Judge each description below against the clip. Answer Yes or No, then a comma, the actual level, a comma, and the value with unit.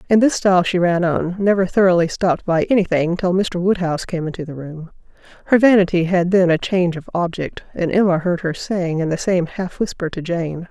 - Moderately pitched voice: Yes, medium, 180 Hz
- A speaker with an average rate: No, fast, 220 wpm